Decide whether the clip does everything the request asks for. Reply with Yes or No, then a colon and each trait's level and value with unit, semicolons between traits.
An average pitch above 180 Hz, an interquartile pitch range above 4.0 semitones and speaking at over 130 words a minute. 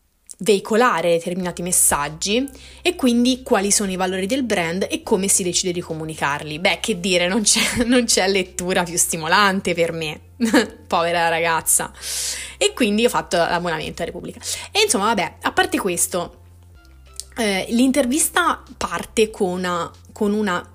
Yes: high, 190 Hz; wide, 5.6 semitones; average, 145 wpm